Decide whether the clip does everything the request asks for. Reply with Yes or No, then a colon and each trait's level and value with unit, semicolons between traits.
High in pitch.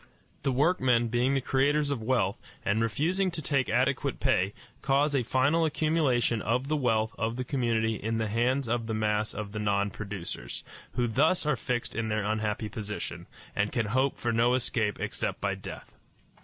No: low, 120 Hz